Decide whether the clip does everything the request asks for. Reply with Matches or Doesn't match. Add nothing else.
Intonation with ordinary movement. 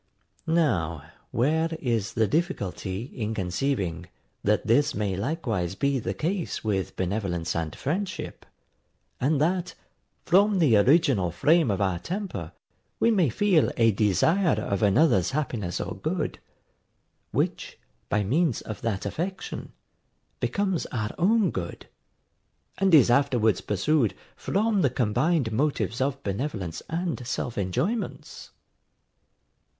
Doesn't match